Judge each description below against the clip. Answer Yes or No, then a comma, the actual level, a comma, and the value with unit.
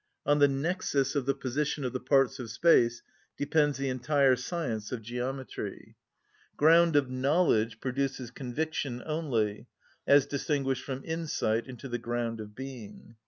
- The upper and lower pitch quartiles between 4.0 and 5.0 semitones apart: No, average, 3.1 semitones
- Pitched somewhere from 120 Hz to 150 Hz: Yes, low, 135 Hz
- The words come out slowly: No, average, 145 wpm